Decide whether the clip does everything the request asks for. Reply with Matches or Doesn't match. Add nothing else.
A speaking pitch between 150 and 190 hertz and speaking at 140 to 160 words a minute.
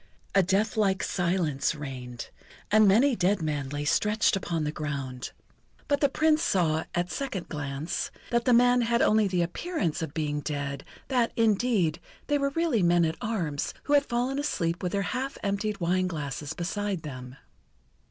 Doesn't match